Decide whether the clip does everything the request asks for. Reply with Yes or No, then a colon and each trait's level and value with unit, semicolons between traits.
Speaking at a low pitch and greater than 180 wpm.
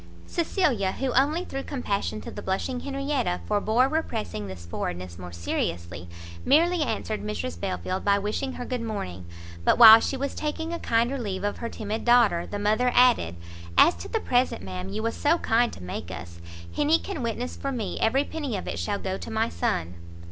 No: high, 225 Hz; average, 190 wpm